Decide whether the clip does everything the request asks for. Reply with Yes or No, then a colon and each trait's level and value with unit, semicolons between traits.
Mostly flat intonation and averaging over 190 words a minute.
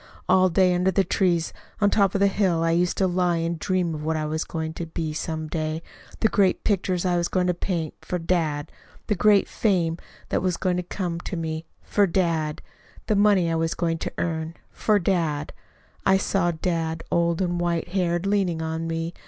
Yes: narrow, 2.3 semitones; average, 200 wpm